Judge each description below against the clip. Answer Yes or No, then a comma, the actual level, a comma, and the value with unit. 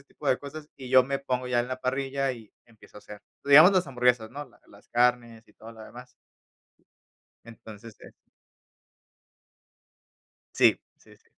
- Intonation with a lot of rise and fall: No, average, 2.9 semitones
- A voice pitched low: Yes, low, 125 Hz